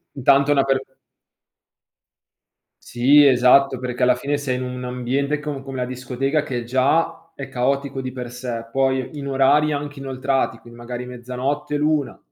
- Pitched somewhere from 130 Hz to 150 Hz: Yes, low, 135 Hz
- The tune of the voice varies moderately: No, narrow, 1.9 semitones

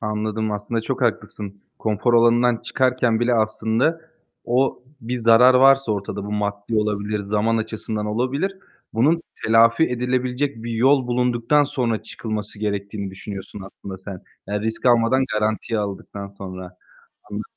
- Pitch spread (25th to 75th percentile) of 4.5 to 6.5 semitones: No, average, 3.0 semitones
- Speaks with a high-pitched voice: No, low, 110 Hz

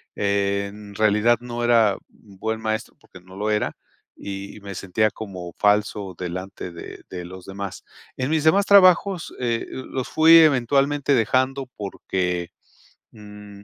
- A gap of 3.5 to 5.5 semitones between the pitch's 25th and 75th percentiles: Yes, average, 4.5 semitones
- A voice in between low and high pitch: No, low, 105 Hz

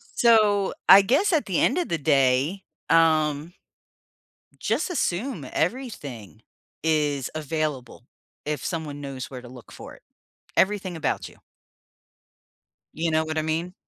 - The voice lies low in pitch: No, medium, 160 Hz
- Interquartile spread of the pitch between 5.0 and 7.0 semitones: Yes, wide, 5.5 semitones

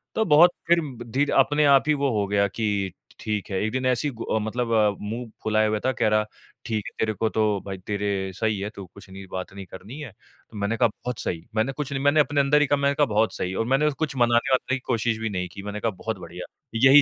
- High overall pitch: No, low, 115 Hz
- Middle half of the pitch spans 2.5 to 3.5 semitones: No, average, 4.8 semitones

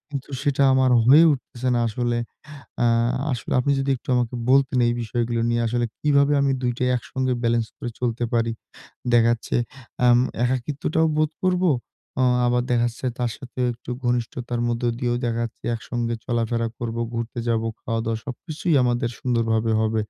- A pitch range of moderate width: No, narrow, 2.0 semitones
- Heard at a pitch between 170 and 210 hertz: No, low, 120 Hz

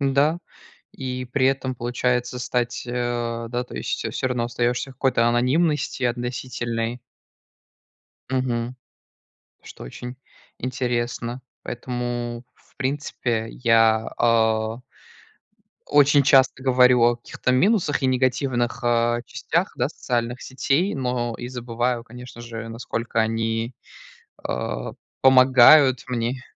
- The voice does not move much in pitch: Yes, narrow, 1.7 semitones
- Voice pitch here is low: Yes, low, 125 Hz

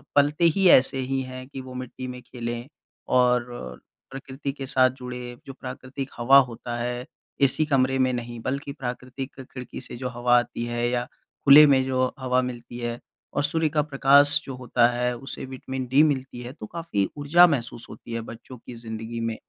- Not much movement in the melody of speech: Yes, narrow, 2.1 semitones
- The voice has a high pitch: No, low, 130 Hz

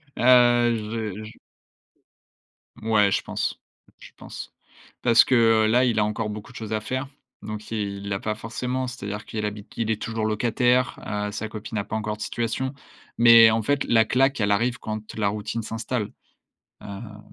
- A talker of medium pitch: No, low, 110 Hz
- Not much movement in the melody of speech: Yes, narrow, 2.0 semitones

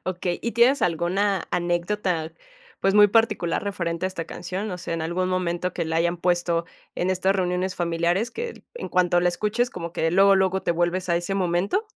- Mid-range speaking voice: Yes, medium, 180 Hz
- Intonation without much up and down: Yes, narrow, 2.2 semitones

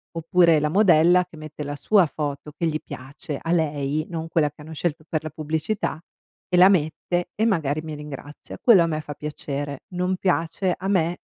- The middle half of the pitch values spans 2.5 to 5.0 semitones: Yes, average, 2.9 semitones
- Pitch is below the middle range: No, medium, 160 Hz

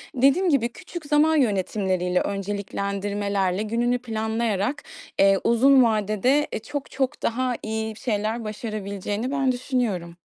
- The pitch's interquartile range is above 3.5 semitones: Yes, average, 4.2 semitones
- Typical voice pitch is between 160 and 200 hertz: No, high, 220 Hz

